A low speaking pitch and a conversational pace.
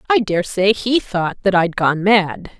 No: high, 200 Hz; average, 185 wpm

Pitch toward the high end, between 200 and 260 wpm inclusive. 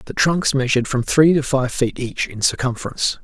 No: low, 130 Hz; fast, 205 wpm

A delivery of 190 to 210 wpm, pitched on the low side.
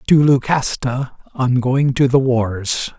No: average, 140 wpm; low, 130 Hz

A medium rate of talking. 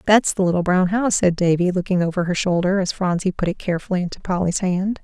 No: fast, 225 wpm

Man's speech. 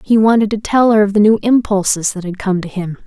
No: female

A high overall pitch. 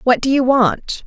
Yes: very high, 250 Hz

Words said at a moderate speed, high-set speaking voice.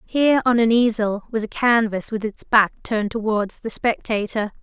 Yes: average, 180 wpm; high, 220 Hz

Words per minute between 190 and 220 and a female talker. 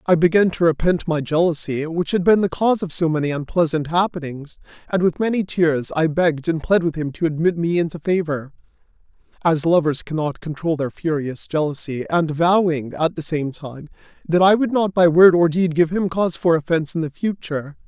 No: average, 200 wpm; male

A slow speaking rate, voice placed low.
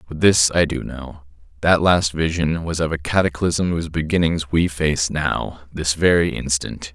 No: average, 155 wpm; very low, 80 Hz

